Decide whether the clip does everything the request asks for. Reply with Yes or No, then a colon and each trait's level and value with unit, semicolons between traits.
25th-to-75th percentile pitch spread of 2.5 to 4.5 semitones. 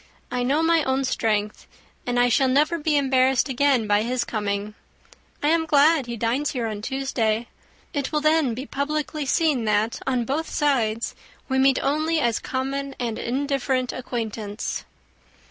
Yes: average, 3.7 semitones